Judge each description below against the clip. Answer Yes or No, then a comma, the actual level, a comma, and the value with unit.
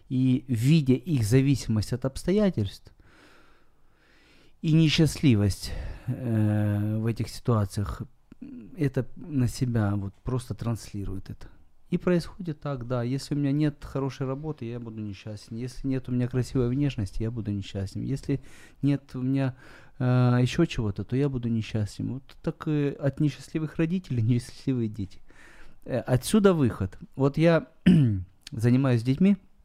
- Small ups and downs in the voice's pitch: No, average, 4.3 semitones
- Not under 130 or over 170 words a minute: Yes, average, 135 wpm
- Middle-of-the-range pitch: No, low, 125 Hz